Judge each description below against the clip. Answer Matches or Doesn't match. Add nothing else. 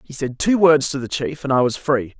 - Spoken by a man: Matches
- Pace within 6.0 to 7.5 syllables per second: Doesn't match